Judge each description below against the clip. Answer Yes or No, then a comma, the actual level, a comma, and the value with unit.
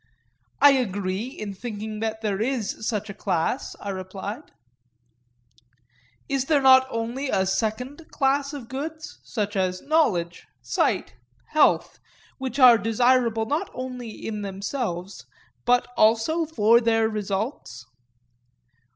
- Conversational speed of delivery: No, slow, 120 wpm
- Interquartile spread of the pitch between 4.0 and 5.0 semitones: Yes, average, 4.5 semitones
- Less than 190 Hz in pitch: No, high, 225 Hz